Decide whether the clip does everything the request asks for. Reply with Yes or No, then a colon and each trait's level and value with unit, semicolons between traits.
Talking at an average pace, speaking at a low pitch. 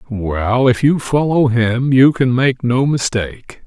Yes: average, 165 wpm; low, 125 Hz